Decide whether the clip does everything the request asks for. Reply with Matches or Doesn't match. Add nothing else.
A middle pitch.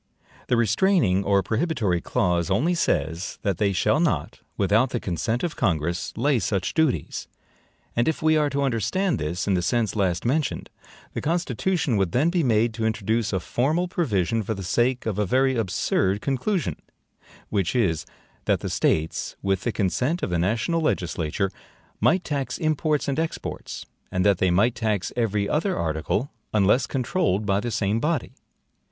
Doesn't match